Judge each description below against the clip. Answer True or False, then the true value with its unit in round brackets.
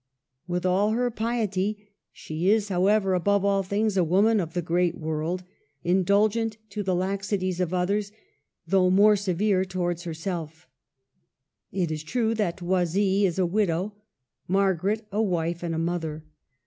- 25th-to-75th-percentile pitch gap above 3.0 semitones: False (2.7 semitones)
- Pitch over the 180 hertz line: True (190 Hz)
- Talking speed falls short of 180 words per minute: True (150 wpm)